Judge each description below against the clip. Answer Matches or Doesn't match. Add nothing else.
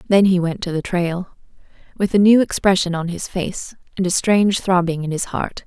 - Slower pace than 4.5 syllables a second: Doesn't match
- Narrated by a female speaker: Matches